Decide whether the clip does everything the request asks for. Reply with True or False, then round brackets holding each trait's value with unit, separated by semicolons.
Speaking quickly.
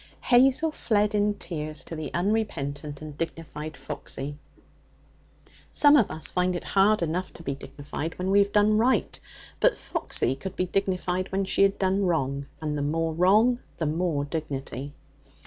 False (165 wpm)